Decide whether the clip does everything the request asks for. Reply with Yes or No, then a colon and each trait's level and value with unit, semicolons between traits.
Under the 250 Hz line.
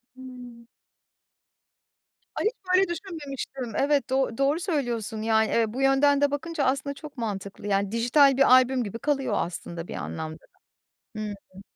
No: very high, 260 Hz